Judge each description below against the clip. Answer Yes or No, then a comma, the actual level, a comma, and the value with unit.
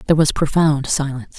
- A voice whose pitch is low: No, medium, 145 Hz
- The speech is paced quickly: No, average, 175 wpm